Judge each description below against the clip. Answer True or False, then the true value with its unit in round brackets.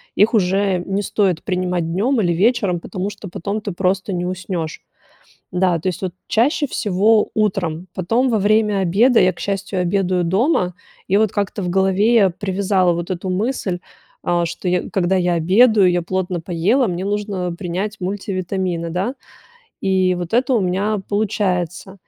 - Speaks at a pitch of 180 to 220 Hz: True (190 Hz)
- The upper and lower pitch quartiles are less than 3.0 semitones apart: True (2.5 semitones)